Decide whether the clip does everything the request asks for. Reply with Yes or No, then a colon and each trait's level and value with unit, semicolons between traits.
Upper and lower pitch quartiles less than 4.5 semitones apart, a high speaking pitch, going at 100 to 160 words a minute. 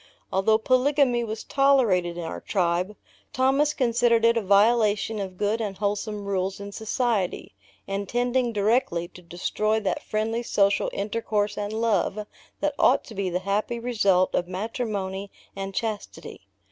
Yes: average, 3.0 semitones; high, 210 Hz; average, 145 wpm